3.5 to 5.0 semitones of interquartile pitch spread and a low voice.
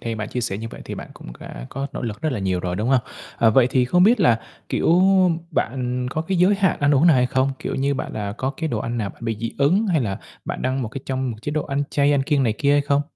Yes: average, 4.2 semitones; low, 130 Hz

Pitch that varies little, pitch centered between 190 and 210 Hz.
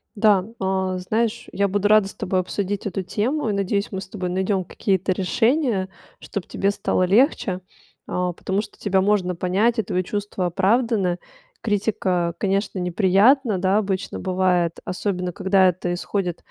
Yes: narrow, 2.1 semitones; high, 195 Hz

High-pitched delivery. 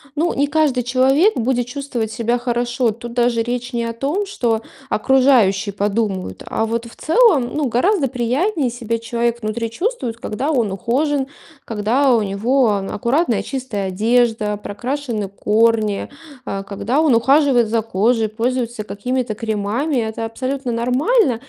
Yes: high, 240 Hz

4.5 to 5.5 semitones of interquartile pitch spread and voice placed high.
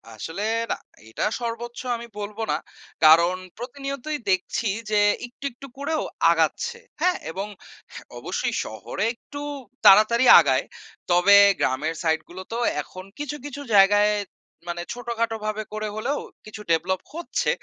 Yes: average, 5.2 semitones; high, 215 Hz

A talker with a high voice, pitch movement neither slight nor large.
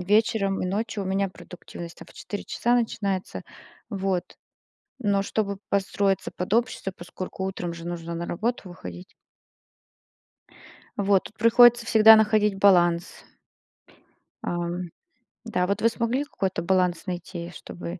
Yes: high, 195 Hz; average, 3.5 semitones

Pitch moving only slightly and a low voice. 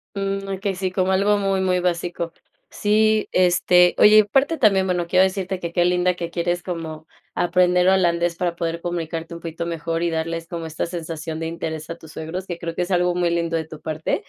No: narrow, 2.0 semitones; medium, 175 Hz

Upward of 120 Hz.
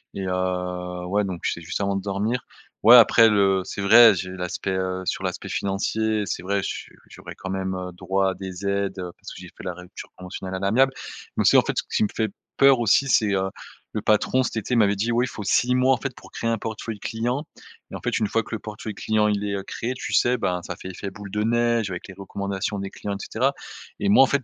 No: low, 100 Hz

